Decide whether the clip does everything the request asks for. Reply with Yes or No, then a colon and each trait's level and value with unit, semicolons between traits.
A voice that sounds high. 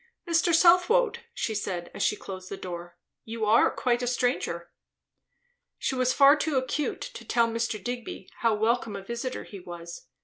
Yes: high, 235 Hz